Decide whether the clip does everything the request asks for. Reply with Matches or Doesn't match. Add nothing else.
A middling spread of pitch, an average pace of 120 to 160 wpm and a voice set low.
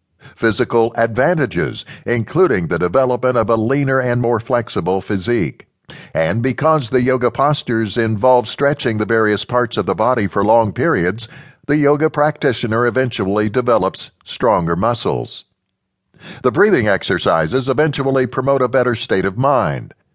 Matches